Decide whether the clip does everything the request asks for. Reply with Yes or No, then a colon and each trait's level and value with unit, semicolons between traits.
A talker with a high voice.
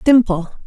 Yes: high, 215 Hz